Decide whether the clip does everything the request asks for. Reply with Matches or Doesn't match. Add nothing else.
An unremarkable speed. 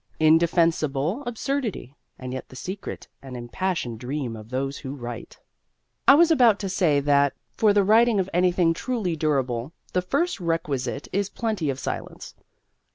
Matches